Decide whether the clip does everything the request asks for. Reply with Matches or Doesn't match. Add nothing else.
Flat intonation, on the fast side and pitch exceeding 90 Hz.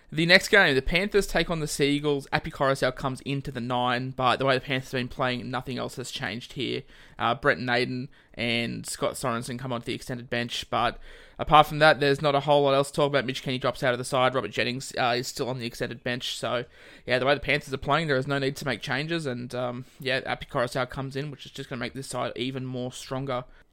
Matches